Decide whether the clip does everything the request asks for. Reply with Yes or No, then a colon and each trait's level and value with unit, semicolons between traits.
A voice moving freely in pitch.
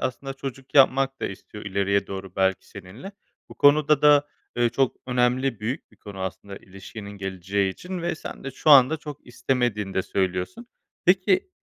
Yes: wide, 6.3 semitones